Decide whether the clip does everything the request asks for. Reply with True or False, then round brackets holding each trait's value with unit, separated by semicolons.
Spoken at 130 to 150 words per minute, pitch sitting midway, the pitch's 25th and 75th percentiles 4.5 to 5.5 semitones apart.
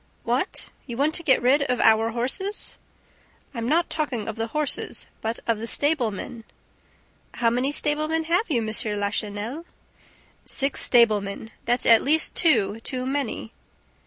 False (145 wpm; 245 Hz; 4.9 semitones)